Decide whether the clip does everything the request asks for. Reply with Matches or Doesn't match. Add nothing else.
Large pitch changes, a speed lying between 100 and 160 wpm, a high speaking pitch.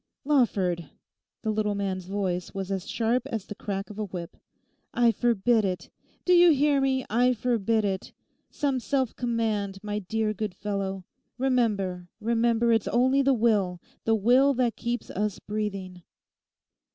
Doesn't match